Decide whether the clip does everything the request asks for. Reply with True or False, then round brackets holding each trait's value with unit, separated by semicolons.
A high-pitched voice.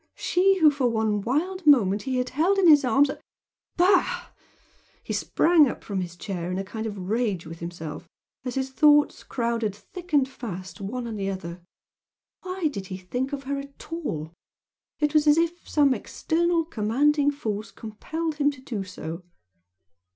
True (255 Hz)